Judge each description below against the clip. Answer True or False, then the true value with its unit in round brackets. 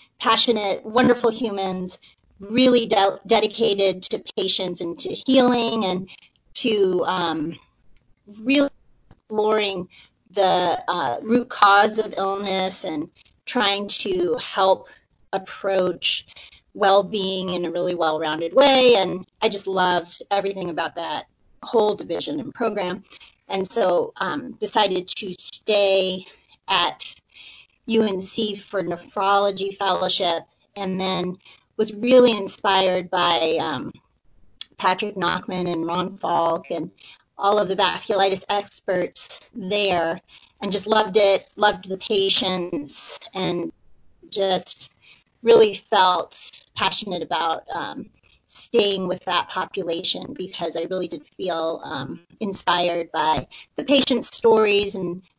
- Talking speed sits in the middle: False (115 wpm)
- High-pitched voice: True (195 Hz)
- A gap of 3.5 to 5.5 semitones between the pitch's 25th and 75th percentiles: False (3.1 semitones)